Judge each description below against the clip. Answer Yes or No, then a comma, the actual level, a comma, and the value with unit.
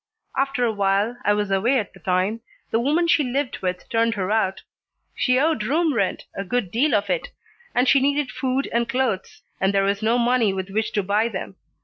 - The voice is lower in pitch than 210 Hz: No, high, 225 Hz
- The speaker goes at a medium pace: No, fast, 215 wpm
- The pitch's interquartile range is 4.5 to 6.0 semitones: Yes, average, 4.8 semitones